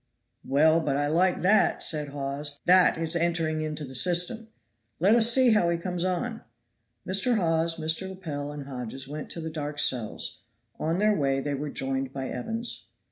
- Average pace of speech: Yes, average, 180 wpm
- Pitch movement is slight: No, average, 4.3 semitones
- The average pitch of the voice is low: No, medium, 160 Hz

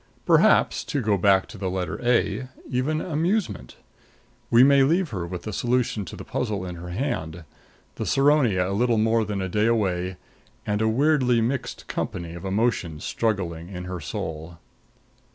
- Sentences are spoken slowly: No, average, 170 wpm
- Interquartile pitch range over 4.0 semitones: Yes, wide, 5.6 semitones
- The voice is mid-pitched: No, low, 105 Hz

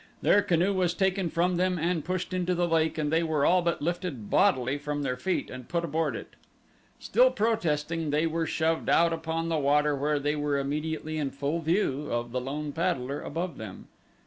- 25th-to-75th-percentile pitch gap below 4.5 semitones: Yes, average, 3.1 semitones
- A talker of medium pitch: Yes, medium, 160 Hz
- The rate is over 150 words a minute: Yes, average, 200 wpm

